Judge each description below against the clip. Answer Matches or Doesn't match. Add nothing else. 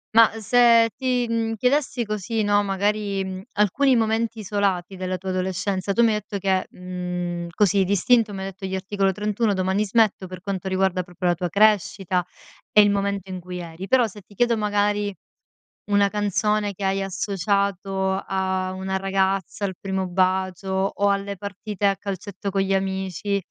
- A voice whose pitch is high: Matches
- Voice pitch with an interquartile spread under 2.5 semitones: Matches